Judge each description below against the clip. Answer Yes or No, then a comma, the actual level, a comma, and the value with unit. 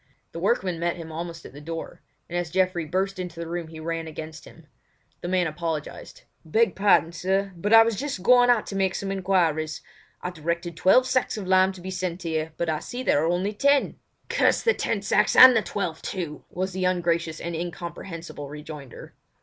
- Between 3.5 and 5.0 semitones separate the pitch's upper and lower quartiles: No, average, 2.9 semitones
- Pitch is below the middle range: No, medium, 175 Hz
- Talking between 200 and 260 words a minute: Yes, fast, 205 wpm